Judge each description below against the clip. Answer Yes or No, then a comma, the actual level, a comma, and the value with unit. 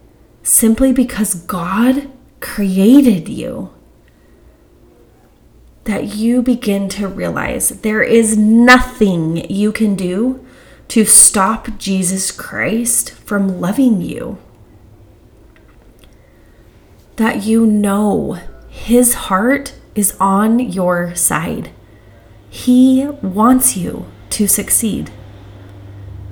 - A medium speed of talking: No, slow, 85 wpm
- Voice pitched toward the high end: Yes, high, 200 Hz